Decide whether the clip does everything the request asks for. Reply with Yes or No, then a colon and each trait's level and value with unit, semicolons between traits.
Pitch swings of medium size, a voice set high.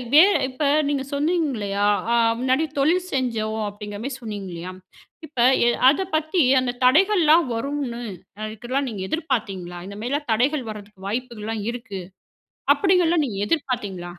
No: wide, 5.9 semitones; high, 245 Hz